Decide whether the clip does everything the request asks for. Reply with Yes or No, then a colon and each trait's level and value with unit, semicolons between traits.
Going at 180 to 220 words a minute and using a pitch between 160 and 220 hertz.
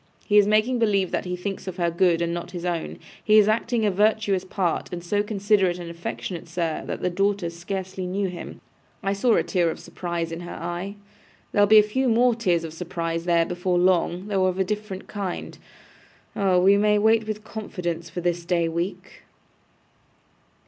Yes: average, 195 wpm; medium, 185 Hz